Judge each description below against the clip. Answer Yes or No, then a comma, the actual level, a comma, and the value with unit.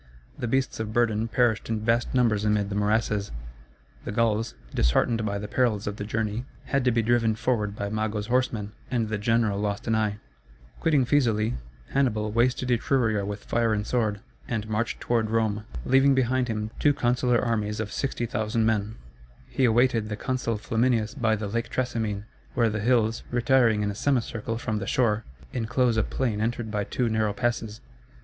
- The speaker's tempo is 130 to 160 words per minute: No, average, 175 wpm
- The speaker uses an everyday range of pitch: No, narrow, 2.2 semitones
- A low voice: Yes, low, 110 Hz